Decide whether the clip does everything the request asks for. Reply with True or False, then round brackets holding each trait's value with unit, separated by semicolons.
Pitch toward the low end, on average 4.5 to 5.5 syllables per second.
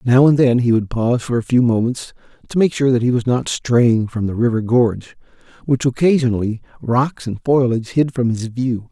True (120 Hz; 5.3 syllables/s)